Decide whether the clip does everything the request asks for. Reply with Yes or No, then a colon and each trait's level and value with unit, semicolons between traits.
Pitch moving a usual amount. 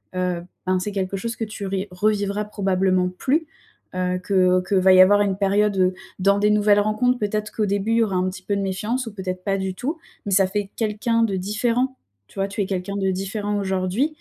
No: narrow, 2.2 semitones